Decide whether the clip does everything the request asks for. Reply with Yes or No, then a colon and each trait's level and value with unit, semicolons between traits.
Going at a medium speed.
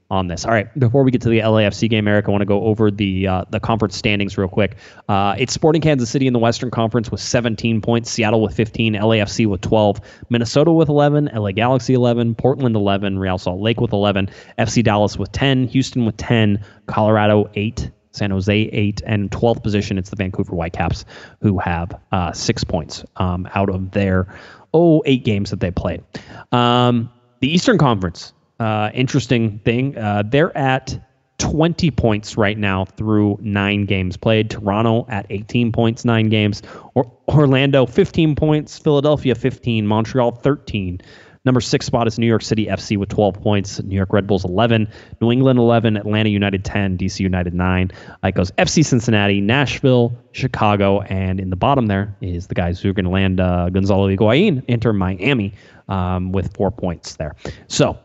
Yes: average, 180 wpm